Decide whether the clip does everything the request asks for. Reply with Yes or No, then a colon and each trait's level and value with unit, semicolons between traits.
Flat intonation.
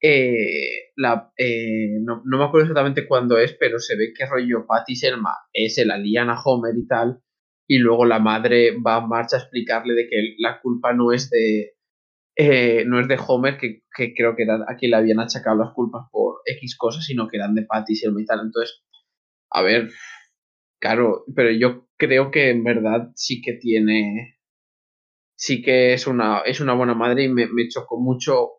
Yes: narrow, 2.2 semitones